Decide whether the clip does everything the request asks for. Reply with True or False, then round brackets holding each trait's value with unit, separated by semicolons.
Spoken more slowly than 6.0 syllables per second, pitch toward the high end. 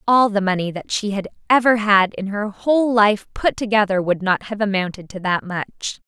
True (5.0 syllables/s; 205 Hz)